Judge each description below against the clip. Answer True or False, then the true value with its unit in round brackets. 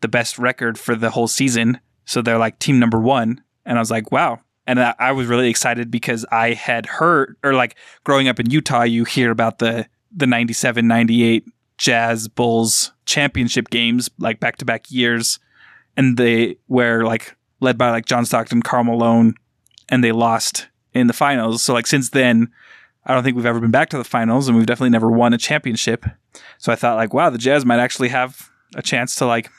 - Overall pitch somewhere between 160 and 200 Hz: False (120 Hz)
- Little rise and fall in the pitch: True (1.5 semitones)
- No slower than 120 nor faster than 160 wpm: False (205 wpm)